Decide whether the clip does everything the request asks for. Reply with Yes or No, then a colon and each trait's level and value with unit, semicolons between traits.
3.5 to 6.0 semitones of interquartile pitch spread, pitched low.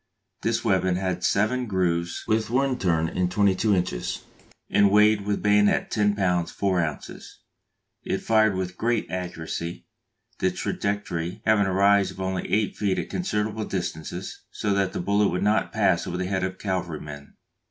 No: narrow, 2.6 semitones; very low, 95 Hz